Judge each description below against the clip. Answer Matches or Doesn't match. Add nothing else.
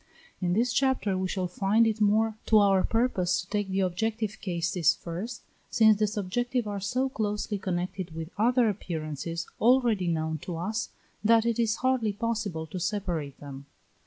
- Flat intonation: Doesn't match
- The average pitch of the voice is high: Matches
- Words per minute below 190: Matches